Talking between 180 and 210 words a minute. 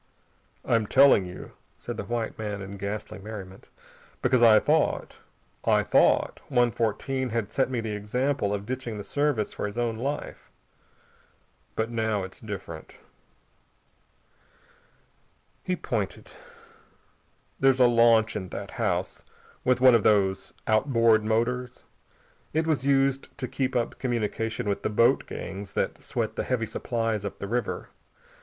No: average, 140 wpm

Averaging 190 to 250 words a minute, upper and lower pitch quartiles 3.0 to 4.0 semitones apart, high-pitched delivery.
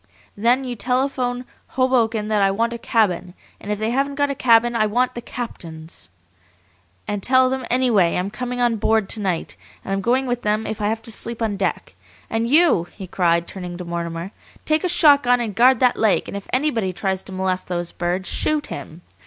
No: fast, 205 wpm; average, 4.7 semitones; high, 225 Hz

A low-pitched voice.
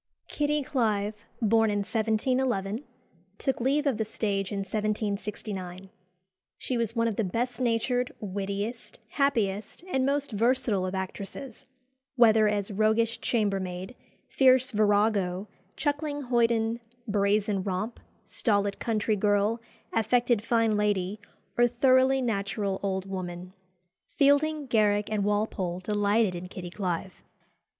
No: high, 215 Hz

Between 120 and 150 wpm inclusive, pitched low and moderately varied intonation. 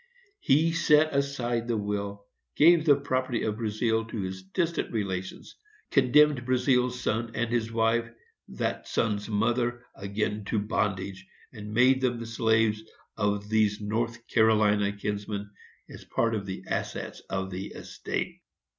Yes: average, 140 wpm; low, 110 Hz; average, 3.0 semitones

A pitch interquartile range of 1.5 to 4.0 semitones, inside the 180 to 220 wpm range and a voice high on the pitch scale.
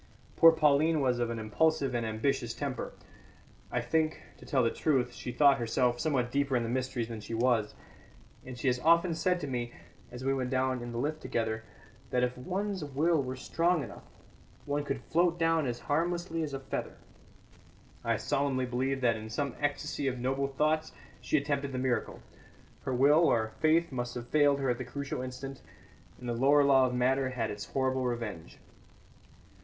No: average, 3.2 semitones; average, 190 wpm; low, 130 Hz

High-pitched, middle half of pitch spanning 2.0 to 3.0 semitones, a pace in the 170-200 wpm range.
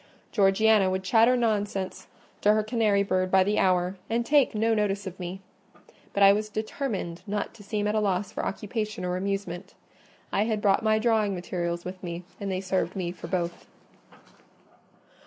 Yes: high, 200 Hz; narrow, 2.6 semitones; average, 175 wpm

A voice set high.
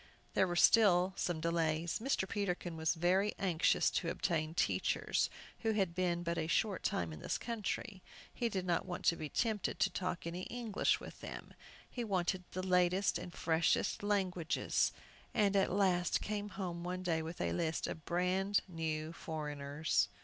No: medium, 180 Hz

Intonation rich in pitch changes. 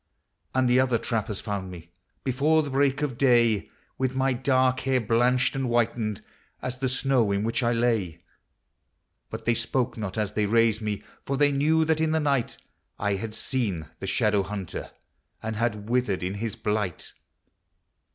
No: average, 3.8 semitones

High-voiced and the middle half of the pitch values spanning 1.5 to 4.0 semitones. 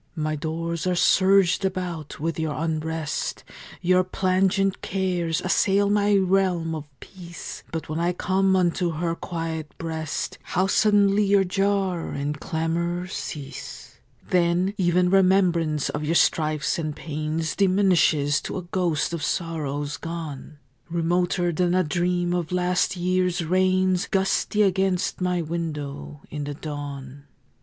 No: medium, 175 Hz; average, 2.9 semitones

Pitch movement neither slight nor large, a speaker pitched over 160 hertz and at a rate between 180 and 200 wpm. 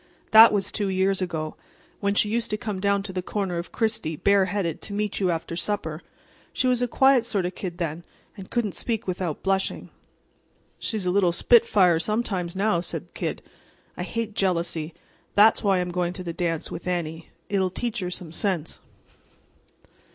Yes: average, 3.3 semitones; high, 190 Hz; average, 190 wpm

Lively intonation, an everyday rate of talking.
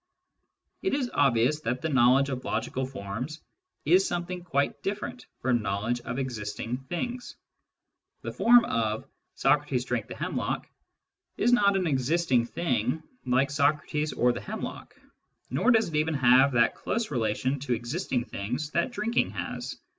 Yes: wide, 5.8 semitones; average, 155 wpm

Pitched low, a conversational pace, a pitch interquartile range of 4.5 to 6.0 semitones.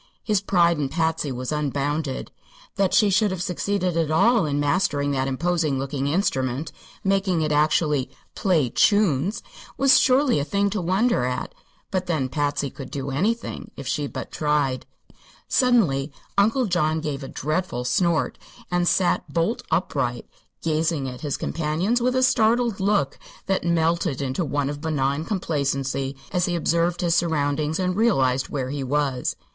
No: medium, 160 Hz; average, 155 wpm; average, 5.1 semitones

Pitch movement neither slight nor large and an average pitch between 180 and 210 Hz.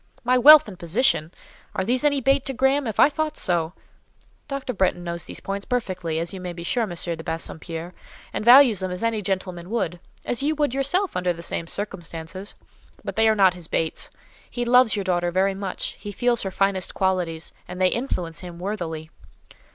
No: wide, 5.8 semitones; high, 190 Hz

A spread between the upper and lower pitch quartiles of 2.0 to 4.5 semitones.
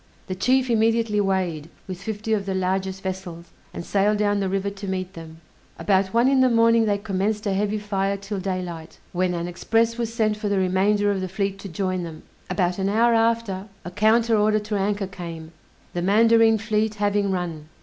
Yes: narrow, 2.5 semitones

